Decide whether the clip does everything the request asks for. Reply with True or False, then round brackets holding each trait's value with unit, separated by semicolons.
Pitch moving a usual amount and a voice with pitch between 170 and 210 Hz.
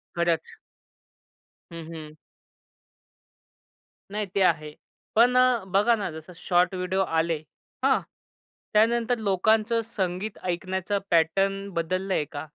True (4.0 semitones; 190 Hz)